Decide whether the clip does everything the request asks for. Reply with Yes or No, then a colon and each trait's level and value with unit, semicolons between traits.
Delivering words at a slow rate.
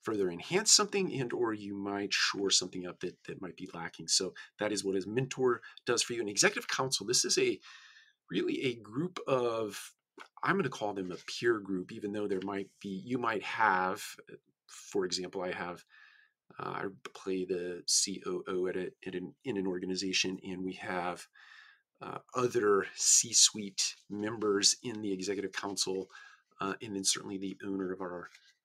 No: average, 180 wpm